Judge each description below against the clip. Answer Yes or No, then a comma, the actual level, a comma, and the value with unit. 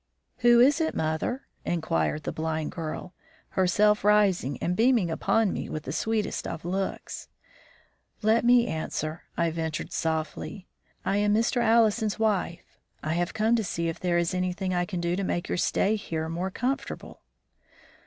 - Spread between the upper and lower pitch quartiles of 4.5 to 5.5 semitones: Yes, average, 4.9 semitones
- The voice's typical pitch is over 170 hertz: Yes, medium, 185 Hz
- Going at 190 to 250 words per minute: No, average, 165 wpm